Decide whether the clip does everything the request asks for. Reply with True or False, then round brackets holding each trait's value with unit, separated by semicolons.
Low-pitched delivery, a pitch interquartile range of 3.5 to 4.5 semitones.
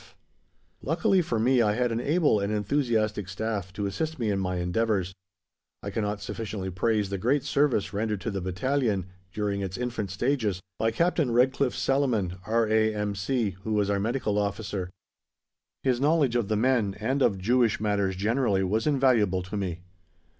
True (110 Hz; 3.9 semitones)